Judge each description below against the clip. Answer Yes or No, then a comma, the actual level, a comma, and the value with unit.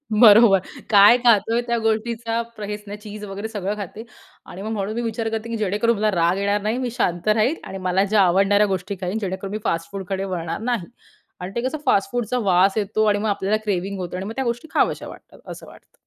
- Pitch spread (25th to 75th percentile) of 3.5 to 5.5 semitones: No, narrow, 2.4 semitones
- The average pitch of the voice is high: Yes, high, 210 Hz